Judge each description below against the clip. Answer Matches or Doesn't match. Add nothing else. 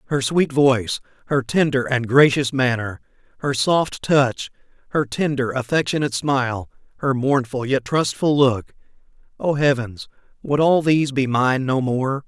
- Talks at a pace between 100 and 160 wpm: Matches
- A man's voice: Matches